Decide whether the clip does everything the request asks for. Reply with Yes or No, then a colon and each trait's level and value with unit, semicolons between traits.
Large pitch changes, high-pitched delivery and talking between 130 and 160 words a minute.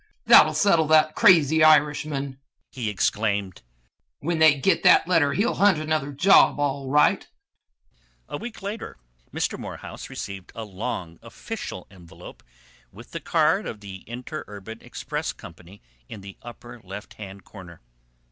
No: wide, 7.4 semitones; low, 135 Hz; average, 140 wpm